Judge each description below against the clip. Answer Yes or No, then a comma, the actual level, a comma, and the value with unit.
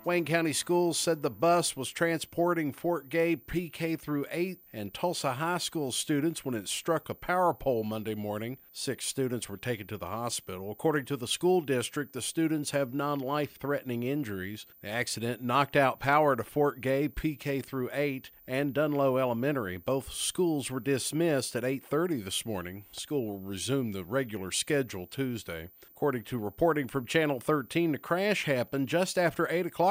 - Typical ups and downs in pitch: Yes, average, 5.0 semitones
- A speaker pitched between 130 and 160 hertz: Yes, medium, 140 Hz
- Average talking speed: Yes, average, 170 wpm